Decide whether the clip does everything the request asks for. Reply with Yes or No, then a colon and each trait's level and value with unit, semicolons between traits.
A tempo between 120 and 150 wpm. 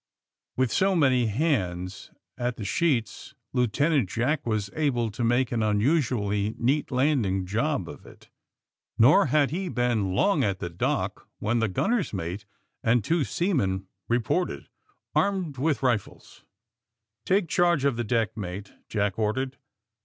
Yes: average, 145 wpm